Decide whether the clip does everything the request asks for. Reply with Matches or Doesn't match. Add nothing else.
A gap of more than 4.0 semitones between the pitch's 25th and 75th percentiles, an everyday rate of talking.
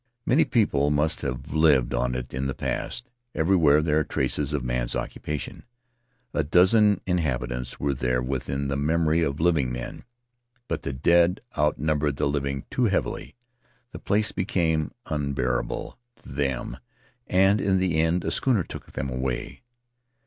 Matches